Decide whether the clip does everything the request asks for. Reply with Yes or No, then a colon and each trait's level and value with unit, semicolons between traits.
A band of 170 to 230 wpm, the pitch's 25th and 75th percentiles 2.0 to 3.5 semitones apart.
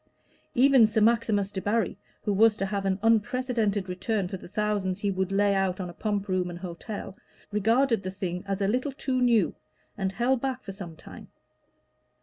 Yes: average, 185 wpm; average, 3.1 semitones